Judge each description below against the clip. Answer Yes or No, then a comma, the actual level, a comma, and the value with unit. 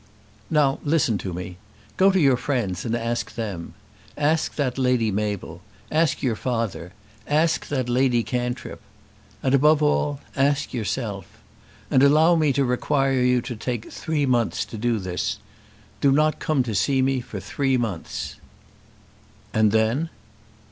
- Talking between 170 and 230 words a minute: No, average, 150 wpm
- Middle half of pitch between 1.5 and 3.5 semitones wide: No, average, 4.2 semitones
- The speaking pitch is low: Yes, low, 125 Hz